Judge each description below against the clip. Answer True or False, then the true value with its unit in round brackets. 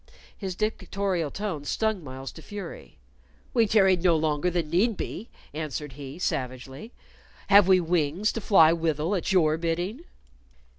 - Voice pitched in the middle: True (175 Hz)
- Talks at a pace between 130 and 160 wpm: True (145 wpm)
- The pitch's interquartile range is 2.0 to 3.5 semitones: False (4.6 semitones)